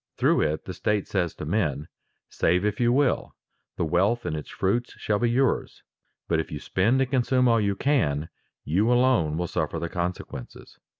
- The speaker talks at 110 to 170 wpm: No, average, 185 wpm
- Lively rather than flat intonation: Yes, wide, 6.8 semitones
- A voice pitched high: No, very low, 95 Hz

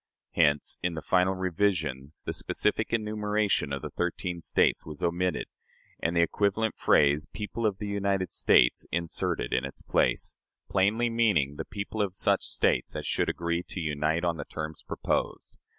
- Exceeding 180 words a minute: No, average, 165 wpm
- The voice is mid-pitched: No, very low, 90 Hz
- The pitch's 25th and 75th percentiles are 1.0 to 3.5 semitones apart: No, average, 4.6 semitones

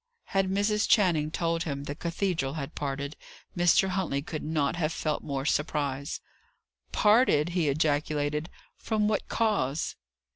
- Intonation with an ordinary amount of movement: Yes, average, 4.5 semitones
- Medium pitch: Yes, medium, 155 Hz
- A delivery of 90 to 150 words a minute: Yes, slow, 135 wpm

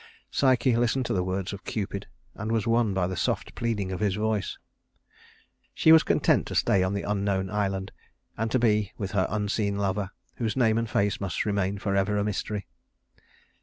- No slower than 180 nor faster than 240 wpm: Yes, average, 185 wpm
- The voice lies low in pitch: Yes, low, 105 Hz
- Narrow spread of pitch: Yes, narrow, 2.3 semitones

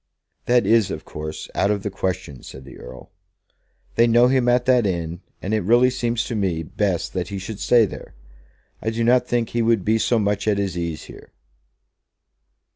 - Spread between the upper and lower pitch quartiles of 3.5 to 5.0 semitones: Yes, average, 4.4 semitones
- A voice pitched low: Yes, low, 105 Hz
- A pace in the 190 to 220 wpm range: Yes, average, 200 wpm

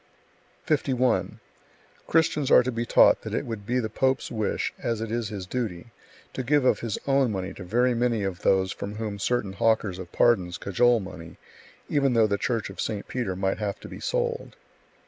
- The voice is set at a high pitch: No, low, 115 Hz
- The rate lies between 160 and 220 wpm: Yes, average, 195 wpm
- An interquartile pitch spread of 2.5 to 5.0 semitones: Yes, average, 4.1 semitones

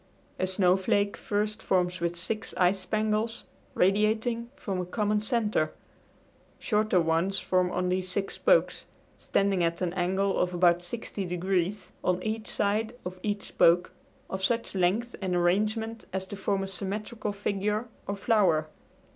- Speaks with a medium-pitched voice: No, high, 195 Hz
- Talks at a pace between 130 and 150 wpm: Yes, average, 145 wpm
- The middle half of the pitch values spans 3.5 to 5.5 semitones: No, average, 2.8 semitones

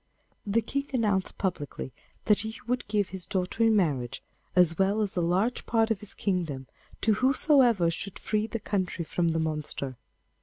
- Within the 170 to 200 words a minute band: Yes, average, 175 wpm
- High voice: Yes, high, 195 Hz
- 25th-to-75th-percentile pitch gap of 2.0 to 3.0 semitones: No, average, 4.6 semitones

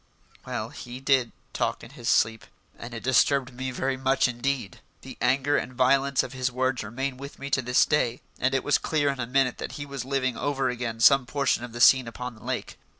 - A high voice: No, low, 130 Hz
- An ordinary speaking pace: No, fast, 220 wpm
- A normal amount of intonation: No, narrow, 2.0 semitones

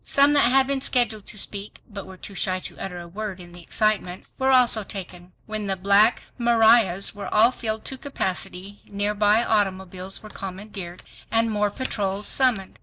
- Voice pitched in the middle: No, high, 205 Hz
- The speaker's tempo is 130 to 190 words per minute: Yes, average, 180 wpm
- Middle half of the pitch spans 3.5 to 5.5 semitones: No, average, 3.0 semitones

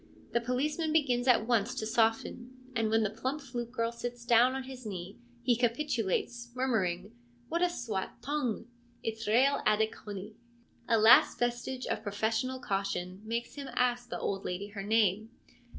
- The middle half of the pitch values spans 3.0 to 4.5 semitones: No, narrow, 2.6 semitones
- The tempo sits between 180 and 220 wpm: No, average, 170 wpm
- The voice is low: No, high, 235 Hz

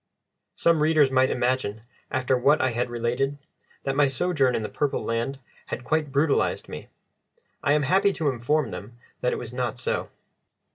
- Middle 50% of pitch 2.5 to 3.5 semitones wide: Yes, average, 3.2 semitones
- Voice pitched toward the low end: Yes, low, 130 Hz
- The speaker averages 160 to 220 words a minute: Yes, average, 175 wpm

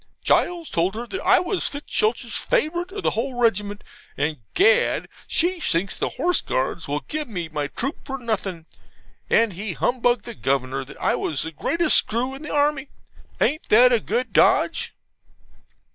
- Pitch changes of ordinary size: No, wide, 8.9 semitones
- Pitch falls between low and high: No, high, 235 Hz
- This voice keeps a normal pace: Yes, average, 170 wpm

